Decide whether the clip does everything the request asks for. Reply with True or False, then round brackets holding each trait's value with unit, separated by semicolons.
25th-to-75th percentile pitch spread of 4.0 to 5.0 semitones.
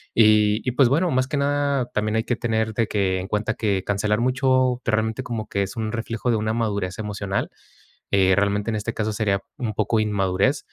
False (2.9 semitones)